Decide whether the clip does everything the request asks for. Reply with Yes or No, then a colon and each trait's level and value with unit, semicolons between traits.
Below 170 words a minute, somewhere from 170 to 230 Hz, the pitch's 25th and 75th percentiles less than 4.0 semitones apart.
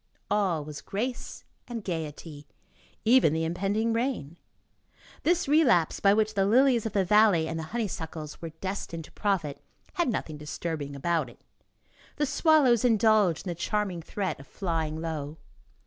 No: average, 150 wpm; high, 190 Hz; wide, 5.6 semitones